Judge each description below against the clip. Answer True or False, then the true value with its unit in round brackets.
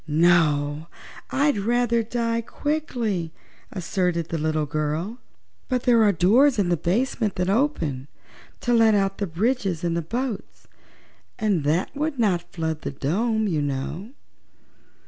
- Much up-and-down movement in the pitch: True (6.4 semitones)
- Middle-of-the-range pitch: False (195 Hz)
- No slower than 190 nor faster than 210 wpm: False (140 wpm)